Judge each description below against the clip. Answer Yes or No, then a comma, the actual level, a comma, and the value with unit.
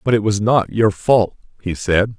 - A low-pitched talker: Yes, low, 105 Hz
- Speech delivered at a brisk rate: Yes, fast, 220 wpm